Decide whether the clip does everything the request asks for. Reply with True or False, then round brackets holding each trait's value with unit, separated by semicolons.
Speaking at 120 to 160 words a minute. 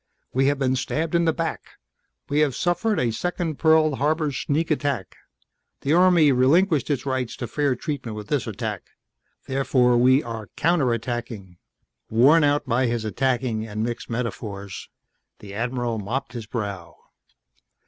True (150 wpm)